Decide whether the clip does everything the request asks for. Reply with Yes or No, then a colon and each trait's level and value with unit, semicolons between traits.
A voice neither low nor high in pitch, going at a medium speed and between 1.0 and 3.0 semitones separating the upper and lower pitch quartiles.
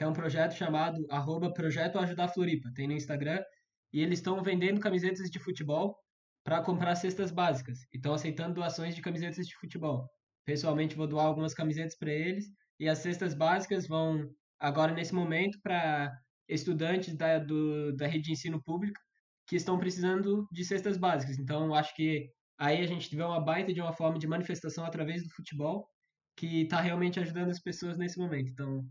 Yes: medium, 165 Hz; average, 175 wpm; narrow, 2.6 semitones